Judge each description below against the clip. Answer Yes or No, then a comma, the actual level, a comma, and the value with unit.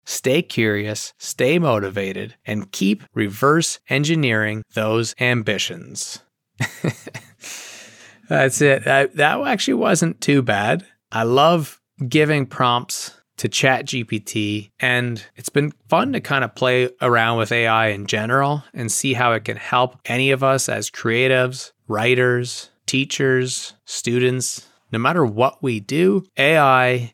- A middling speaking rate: No, slow, 130 wpm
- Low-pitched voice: Yes, low, 125 Hz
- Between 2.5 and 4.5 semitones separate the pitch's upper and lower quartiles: Yes, average, 3.5 semitones